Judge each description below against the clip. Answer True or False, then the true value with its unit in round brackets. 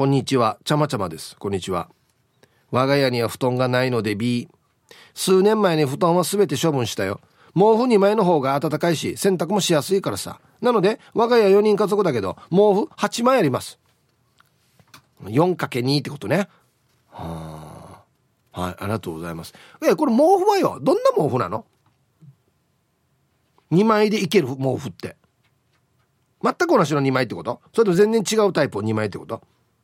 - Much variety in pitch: True (8.3 semitones)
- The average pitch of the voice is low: False (150 Hz)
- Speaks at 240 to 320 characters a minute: True (305 characters per minute)